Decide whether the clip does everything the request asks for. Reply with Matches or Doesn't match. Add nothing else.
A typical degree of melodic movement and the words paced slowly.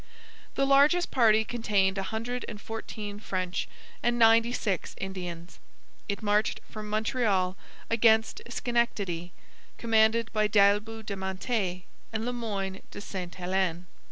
Matches